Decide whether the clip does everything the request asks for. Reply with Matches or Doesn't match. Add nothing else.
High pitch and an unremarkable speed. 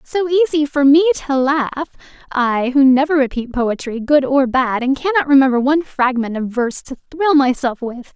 Matches